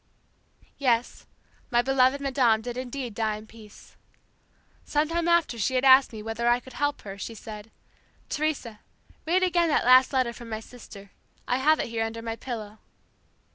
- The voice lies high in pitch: Yes, high, 245 Hz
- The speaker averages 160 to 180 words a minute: Yes, average, 170 wpm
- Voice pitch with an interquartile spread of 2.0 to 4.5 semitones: Yes, average, 3.4 semitones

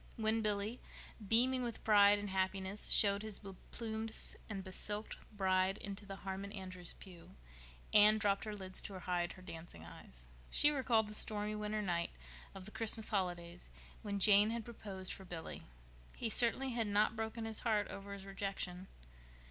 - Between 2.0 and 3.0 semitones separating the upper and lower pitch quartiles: Yes, narrow, 2.4 semitones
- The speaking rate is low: No, average, 170 wpm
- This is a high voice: Yes, high, 205 Hz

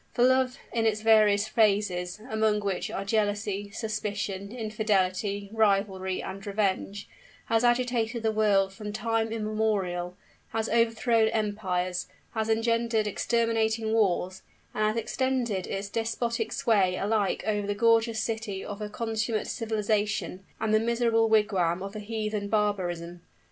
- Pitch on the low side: No, high, 215 Hz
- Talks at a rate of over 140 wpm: No, slow, 135 wpm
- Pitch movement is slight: Yes, narrow, 2.1 semitones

